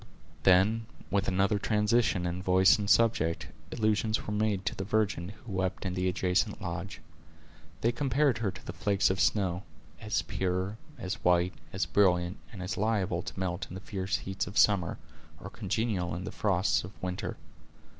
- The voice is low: Yes, very low, 95 Hz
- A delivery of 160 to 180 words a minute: Yes, average, 170 wpm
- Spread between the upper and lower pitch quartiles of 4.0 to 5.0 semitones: No, narrow, 2.6 semitones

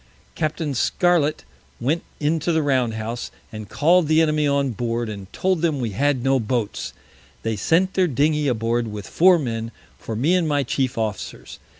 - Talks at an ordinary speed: Yes, average, 175 wpm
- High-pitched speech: No, low, 135 Hz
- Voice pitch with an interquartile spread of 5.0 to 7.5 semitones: Yes, wide, 5.6 semitones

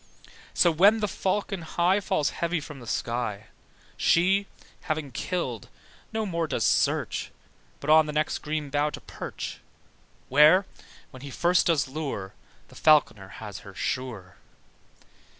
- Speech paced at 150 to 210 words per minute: No, average, 140 wpm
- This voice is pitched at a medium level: Yes, medium, 155 Hz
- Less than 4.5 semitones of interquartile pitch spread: No, average, 5.3 semitones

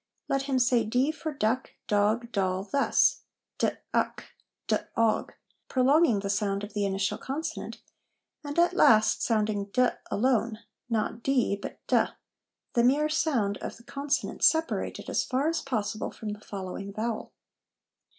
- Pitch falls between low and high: No, high, 230 Hz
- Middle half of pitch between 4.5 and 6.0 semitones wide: Yes, average, 4.9 semitones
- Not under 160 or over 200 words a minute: No, average, 145 wpm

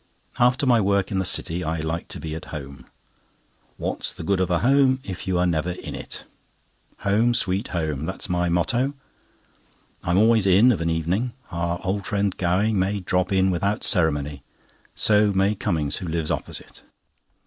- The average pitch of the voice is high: No, very low, 95 Hz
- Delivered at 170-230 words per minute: Yes, average, 180 wpm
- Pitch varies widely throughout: No, average, 3.6 semitones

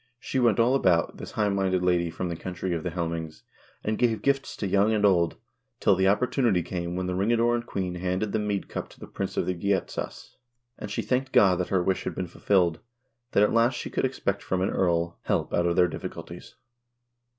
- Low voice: Yes, very low, 95 Hz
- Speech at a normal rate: No, fast, 225 wpm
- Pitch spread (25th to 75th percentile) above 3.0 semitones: Yes, average, 3.4 semitones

